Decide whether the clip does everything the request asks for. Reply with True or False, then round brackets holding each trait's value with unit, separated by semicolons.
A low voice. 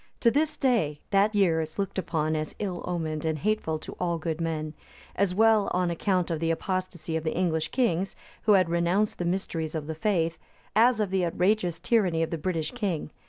False (175 Hz)